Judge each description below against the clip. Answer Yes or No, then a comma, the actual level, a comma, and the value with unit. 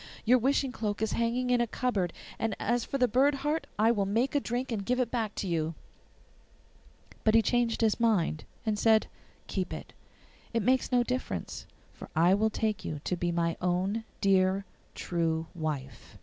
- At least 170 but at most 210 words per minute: Yes, average, 185 wpm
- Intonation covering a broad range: No, average, 4.7 semitones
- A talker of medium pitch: No, high, 220 Hz